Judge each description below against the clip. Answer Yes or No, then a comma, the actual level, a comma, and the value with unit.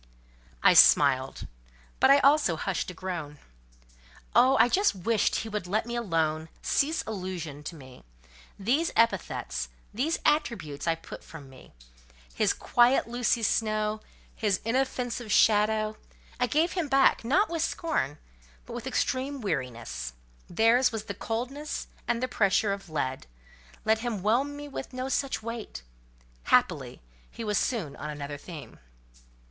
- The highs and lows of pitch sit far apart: Yes, wide, 7.4 semitones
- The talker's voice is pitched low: No, high, 220 Hz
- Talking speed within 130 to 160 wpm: Yes, average, 140 wpm